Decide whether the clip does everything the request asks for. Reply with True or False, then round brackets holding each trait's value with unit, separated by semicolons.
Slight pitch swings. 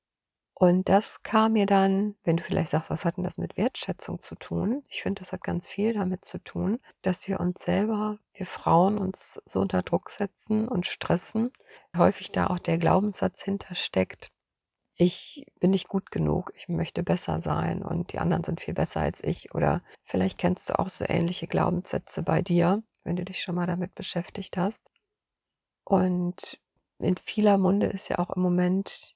True (2.3 semitones)